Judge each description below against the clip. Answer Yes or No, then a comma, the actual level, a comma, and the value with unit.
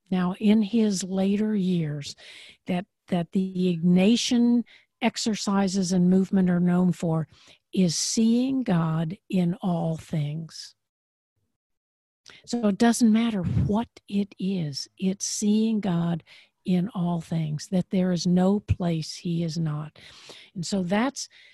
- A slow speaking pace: Yes, slow, 125 wpm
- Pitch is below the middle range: No, medium, 185 Hz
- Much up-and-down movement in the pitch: No, average, 3.7 semitones